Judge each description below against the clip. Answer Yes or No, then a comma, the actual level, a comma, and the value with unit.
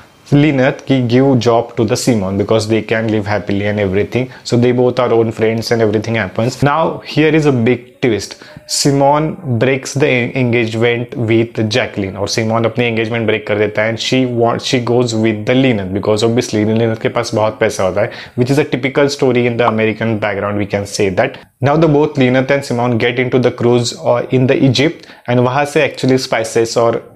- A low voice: Yes, low, 120 Hz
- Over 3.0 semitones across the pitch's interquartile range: No, average, 2.7 semitones